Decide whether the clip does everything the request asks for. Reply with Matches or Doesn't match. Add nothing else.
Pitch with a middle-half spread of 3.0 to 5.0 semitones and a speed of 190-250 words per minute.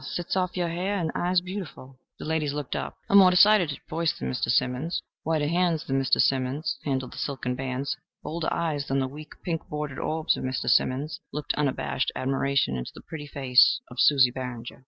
Matches